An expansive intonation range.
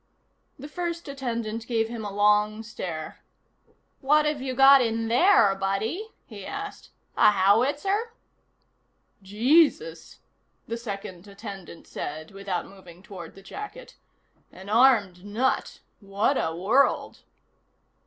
Yes: wide, 5.7 semitones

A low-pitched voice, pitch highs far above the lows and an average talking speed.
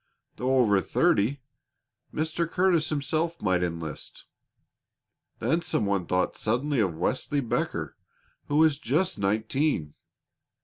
No: low, 130 Hz; wide, 7.8 semitones; slow, 115 wpm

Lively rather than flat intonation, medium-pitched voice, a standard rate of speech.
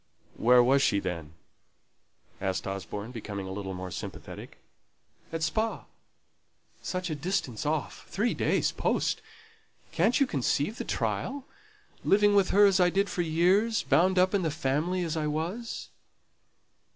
Yes: wide, 8.1 semitones; medium, 160 Hz; average, 145 wpm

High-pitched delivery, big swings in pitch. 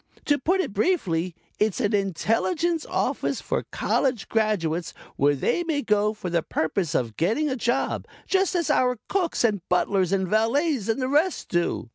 Yes: high, 220 Hz; wide, 8.1 semitones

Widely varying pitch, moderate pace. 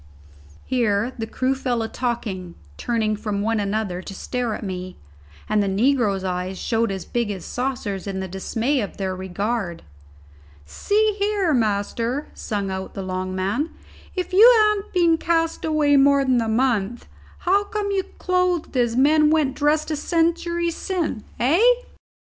Yes: wide, 7.7 semitones; average, 160 wpm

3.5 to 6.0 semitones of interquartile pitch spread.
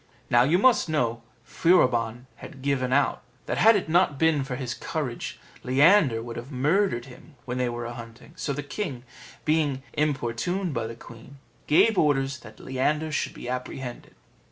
Yes: average, 4.5 semitones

